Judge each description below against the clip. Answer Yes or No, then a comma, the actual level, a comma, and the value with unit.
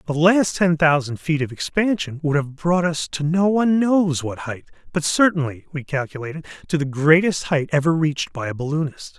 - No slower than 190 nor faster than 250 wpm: Yes, average, 195 wpm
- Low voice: No, medium, 155 Hz